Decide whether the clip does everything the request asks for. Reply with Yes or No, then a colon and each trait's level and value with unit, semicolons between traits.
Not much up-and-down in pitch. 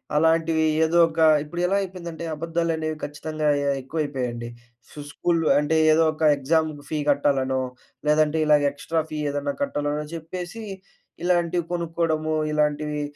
Yes: narrow, 2.0 semitones